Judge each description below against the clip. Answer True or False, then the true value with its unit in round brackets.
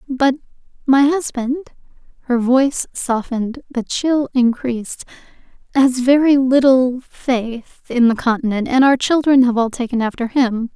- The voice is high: True (255 Hz)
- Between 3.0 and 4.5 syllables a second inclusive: True (4.4 syllables/s)